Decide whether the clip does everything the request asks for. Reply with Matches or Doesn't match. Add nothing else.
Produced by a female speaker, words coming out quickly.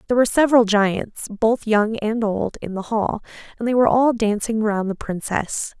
Doesn't match